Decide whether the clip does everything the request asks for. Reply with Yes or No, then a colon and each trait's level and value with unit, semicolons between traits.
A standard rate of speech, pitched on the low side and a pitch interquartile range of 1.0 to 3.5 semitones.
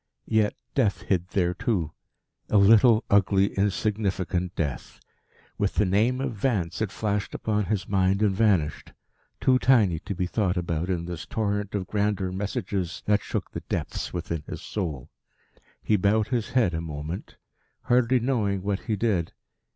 Yes: average, 160 wpm; low, 100 Hz; average, 3.1 semitones